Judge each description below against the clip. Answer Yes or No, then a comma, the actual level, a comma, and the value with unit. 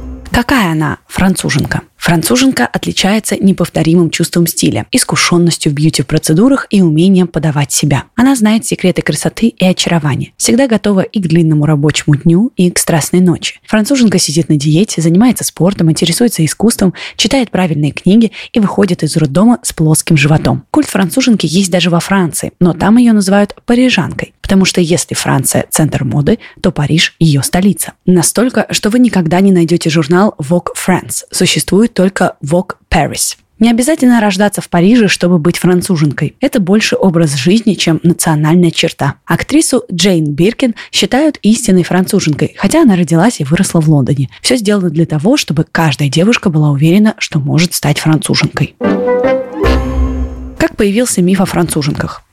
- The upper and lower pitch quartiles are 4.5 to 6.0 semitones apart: Yes, average, 4.8 semitones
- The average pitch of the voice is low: No, medium, 180 Hz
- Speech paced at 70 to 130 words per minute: No, average, 150 wpm